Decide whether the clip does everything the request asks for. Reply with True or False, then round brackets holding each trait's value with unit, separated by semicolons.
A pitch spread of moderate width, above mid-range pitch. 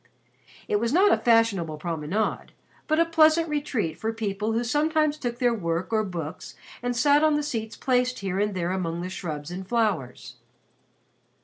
False (7.1 semitones; 225 Hz)